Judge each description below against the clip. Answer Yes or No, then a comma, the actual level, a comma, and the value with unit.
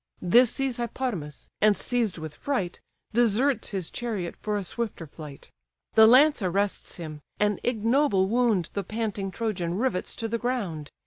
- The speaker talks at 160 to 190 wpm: No, average, 150 wpm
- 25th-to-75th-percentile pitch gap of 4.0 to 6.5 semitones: Yes, average, 4.9 semitones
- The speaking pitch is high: Yes, high, 210 Hz